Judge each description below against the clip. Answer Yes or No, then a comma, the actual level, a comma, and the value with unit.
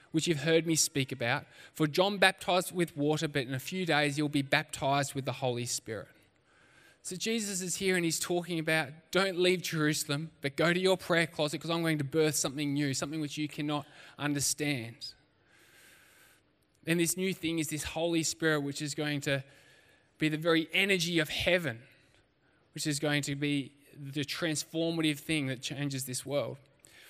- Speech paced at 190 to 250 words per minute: No, average, 180 wpm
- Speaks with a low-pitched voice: No, medium, 150 Hz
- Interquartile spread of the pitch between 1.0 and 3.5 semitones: Yes, average, 2.8 semitones